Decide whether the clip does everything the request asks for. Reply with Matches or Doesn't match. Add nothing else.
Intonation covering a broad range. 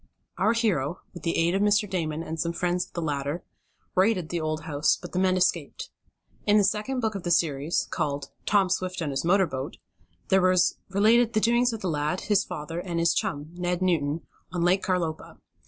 Doesn't match